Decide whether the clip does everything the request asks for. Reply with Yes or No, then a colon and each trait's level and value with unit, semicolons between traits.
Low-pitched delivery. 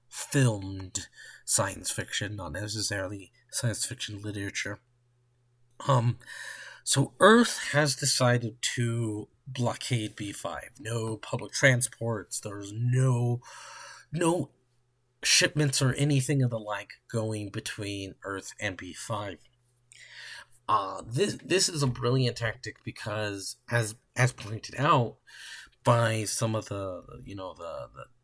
Yes: low, 120 Hz